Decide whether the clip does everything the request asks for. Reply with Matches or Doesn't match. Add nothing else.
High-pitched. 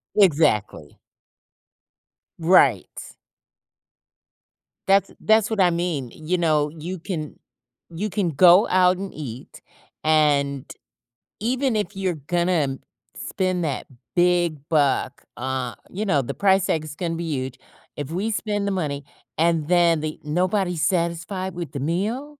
Doesn't match